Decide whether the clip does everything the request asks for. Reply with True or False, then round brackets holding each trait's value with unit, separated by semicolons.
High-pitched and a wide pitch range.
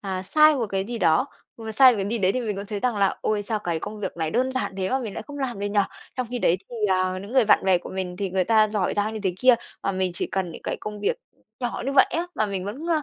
False (210 Hz; 4.3 semitones)